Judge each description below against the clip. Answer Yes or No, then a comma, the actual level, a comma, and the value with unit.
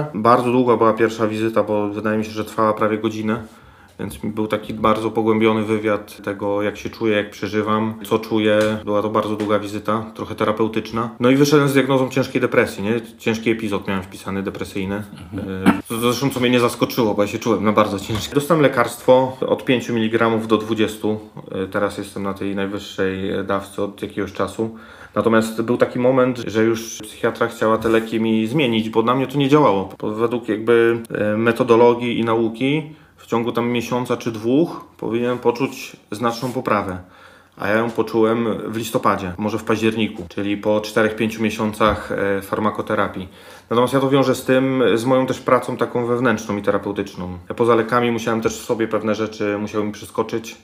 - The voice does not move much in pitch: Yes, narrow, 2.2 semitones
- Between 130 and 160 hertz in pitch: No, low, 110 Hz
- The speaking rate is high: Yes, fast, 175 wpm